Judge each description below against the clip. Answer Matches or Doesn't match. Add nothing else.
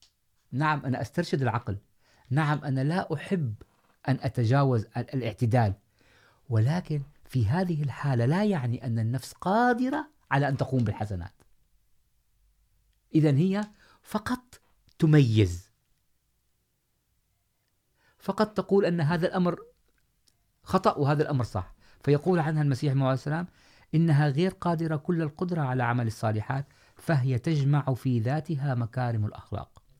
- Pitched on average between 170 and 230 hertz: Doesn't match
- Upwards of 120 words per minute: Doesn't match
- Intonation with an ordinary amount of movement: Doesn't match